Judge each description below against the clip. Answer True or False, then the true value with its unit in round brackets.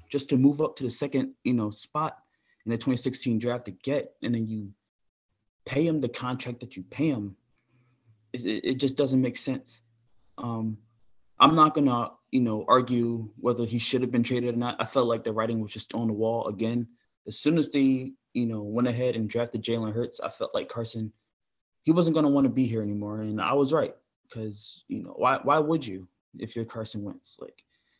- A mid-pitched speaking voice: False (120 Hz)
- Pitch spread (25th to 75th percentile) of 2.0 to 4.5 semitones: True (2.7 semitones)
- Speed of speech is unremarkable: False (210 wpm)